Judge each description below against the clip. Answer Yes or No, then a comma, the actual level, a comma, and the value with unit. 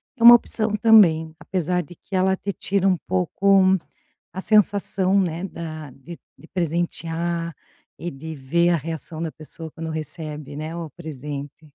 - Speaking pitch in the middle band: Yes, medium, 170 Hz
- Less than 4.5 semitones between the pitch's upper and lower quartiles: Yes, average, 3.1 semitones